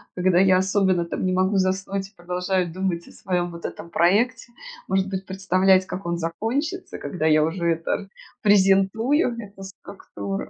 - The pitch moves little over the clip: Yes, narrow, 1.8 semitones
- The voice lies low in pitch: No, high, 190 Hz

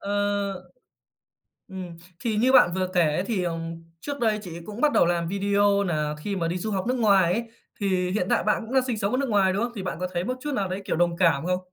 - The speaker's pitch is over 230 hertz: No, high, 195 Hz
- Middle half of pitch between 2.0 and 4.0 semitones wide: Yes, average, 3.4 semitones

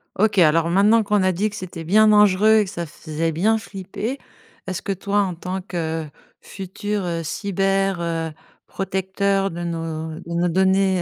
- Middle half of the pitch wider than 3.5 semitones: No, average, 2.9 semitones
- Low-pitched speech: No, high, 190 Hz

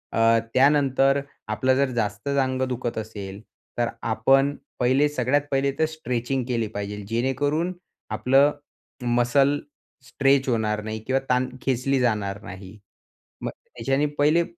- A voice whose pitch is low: Yes, low, 130 Hz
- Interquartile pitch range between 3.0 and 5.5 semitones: Yes, average, 3.5 semitones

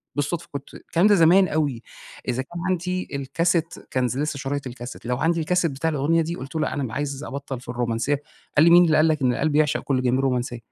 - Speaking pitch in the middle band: Yes, medium, 145 Hz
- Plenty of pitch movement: No, average, 4.0 semitones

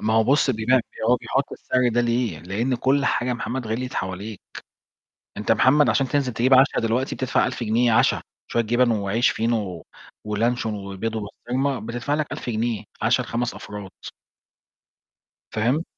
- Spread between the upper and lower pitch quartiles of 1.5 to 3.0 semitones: Yes, average, 2.7 semitones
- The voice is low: Yes, low, 120 Hz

